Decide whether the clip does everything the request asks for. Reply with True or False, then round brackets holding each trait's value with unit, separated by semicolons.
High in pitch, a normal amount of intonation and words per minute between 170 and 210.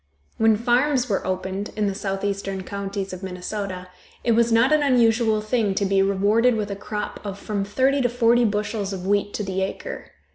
True (205 Hz; 3.0 semitones; 190 wpm)